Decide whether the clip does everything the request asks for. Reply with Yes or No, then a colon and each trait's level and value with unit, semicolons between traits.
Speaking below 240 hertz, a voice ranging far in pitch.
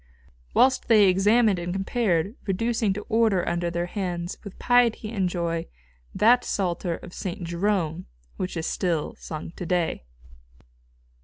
No: medium, 185 Hz; average, 3.8 semitones